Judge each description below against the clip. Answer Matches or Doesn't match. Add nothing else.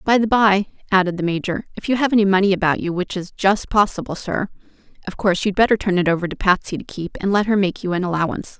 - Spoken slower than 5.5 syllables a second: Doesn't match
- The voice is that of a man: Doesn't match